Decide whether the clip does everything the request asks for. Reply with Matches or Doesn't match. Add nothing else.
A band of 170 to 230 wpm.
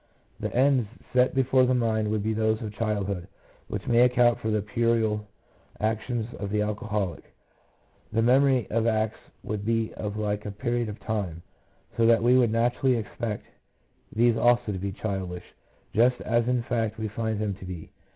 Matches